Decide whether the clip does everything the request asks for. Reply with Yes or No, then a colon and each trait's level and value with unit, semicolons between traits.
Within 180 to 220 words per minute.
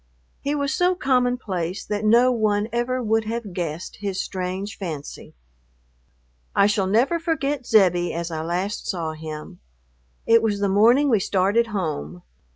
No: average, 155 wpm